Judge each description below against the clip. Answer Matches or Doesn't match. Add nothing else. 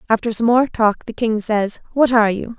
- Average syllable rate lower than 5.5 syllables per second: Matches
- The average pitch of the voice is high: Matches